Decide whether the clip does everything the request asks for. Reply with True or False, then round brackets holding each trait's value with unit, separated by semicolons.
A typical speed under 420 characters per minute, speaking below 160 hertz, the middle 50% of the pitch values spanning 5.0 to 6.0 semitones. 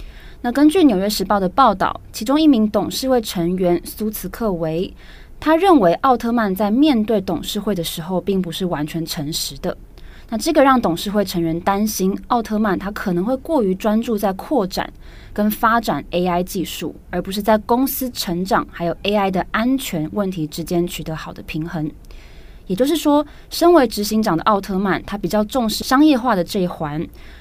False (280 characters per minute; 205 Hz; 5.3 semitones)